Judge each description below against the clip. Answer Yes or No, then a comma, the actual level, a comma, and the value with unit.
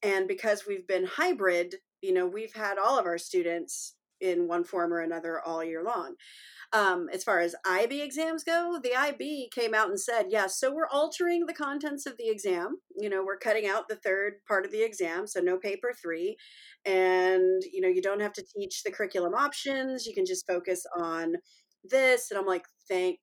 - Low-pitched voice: No, high, 200 Hz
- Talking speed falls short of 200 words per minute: No, fast, 205 wpm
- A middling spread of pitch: No, wide, 7.2 semitones